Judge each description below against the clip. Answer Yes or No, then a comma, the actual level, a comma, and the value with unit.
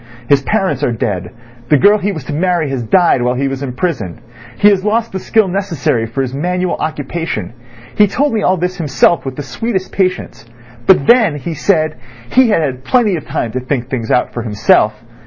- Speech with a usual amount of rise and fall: No, wide, 6.8 semitones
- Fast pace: Yes, fast, 210 wpm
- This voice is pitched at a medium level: Yes, medium, 155 Hz